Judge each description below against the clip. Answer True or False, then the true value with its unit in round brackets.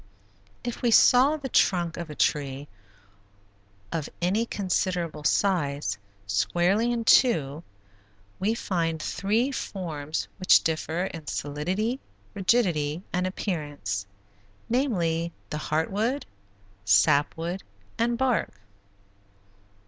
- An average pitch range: False (6.3 semitones)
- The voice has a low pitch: False (175 Hz)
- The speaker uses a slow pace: True (105 wpm)